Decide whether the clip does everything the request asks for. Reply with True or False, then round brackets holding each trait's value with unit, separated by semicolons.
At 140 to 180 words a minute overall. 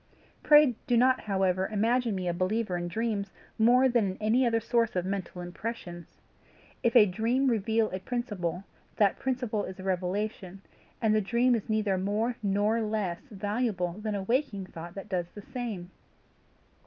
True (165 wpm)